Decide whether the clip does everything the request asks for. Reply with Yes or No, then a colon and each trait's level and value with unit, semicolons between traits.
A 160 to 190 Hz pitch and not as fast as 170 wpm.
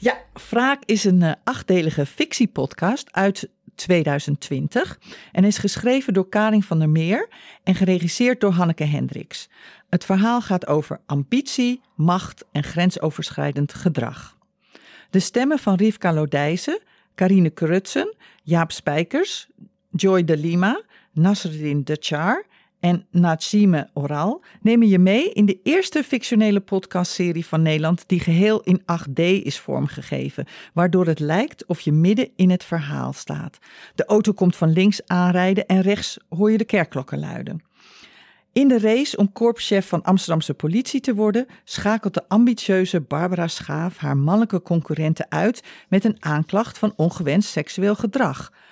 Yes: medium, 185 Hz; average, 140 wpm